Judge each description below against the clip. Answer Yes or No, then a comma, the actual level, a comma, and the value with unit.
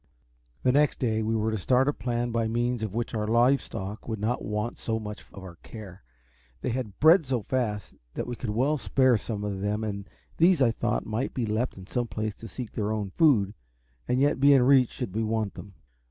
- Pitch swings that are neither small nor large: Yes, average, 3.1 semitones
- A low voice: Yes, low, 115 Hz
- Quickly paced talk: Yes, fast, 225 wpm